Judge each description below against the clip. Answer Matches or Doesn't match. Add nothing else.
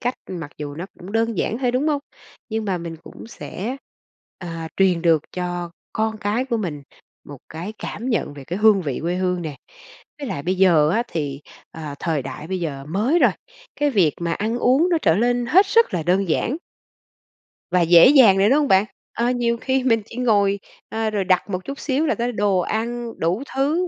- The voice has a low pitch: Doesn't match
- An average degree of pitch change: Doesn't match